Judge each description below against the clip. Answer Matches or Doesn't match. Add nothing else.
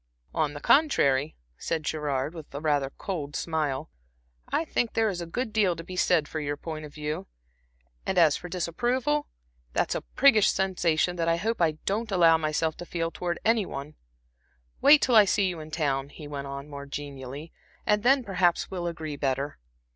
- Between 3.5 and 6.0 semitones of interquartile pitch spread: Matches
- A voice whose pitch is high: Doesn't match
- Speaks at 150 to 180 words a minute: Doesn't match